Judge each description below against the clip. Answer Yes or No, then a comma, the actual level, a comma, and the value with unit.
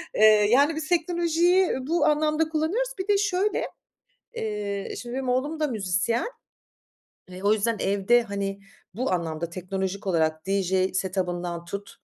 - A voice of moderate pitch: No, high, 215 Hz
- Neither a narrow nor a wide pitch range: No, wide, 8.5 semitones